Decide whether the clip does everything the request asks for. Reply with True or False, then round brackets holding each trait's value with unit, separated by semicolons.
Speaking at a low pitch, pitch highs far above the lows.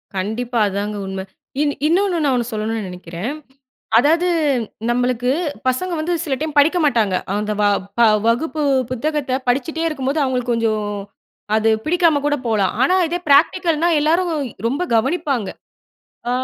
False (260 Hz; 5.9 semitones)